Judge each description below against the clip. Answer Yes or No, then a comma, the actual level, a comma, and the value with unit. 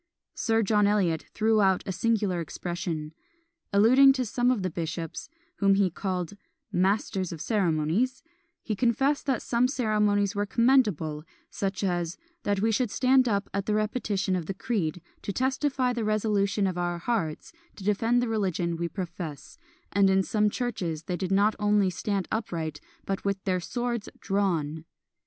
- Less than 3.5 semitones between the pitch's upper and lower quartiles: No, average, 3.9 semitones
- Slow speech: No, average, 160 wpm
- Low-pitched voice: No, high, 200 Hz